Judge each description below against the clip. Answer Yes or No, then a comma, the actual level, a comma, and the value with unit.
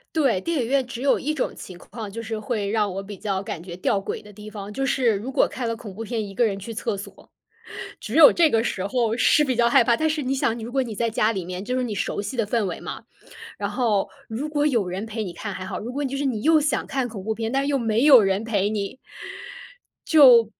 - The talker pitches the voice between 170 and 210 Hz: No, high, 225 Hz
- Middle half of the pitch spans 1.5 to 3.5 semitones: No, average, 4.2 semitones